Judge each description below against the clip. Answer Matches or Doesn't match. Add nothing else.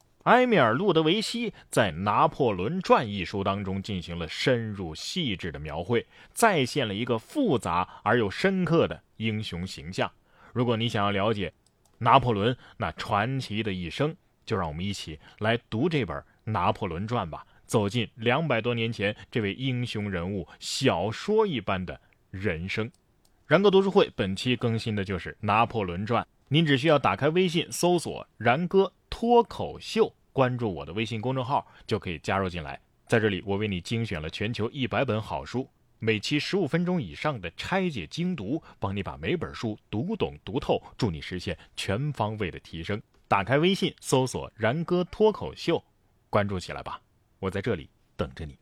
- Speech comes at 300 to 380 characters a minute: Doesn't match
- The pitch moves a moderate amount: Doesn't match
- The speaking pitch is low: Matches